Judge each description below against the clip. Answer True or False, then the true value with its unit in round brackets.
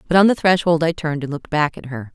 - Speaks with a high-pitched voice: False (155 Hz)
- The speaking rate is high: True (305 wpm)